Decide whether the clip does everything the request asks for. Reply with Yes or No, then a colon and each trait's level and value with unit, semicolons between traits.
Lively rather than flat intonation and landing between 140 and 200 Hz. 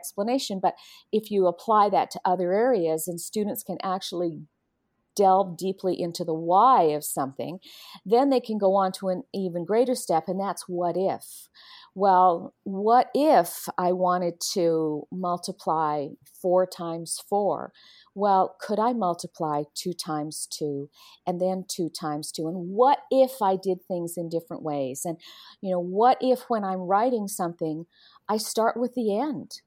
No: average, 3.3 semitones; medium, 185 Hz